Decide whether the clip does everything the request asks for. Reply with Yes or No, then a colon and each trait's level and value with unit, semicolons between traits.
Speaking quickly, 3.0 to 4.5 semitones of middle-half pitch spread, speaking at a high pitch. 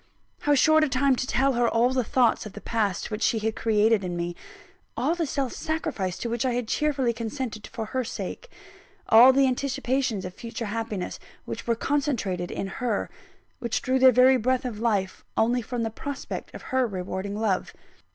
No: average, 190 wpm; average, 3.5 semitones; high, 235 Hz